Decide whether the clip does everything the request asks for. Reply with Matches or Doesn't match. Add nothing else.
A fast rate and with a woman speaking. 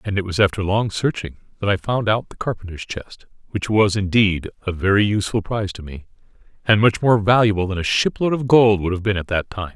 Doesn't match